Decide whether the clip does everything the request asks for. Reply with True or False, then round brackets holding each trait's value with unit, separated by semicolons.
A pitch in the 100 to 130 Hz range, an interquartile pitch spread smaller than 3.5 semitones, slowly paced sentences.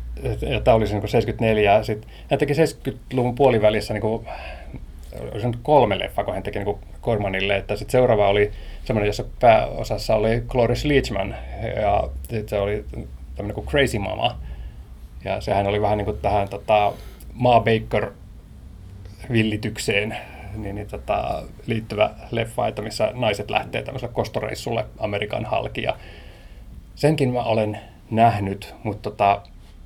False (105 Hz; 2.8 semitones; 135 wpm)